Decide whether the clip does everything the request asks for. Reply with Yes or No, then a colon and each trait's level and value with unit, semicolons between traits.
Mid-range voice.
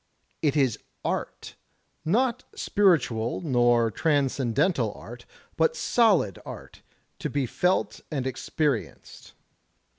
Yes: medium, 145 Hz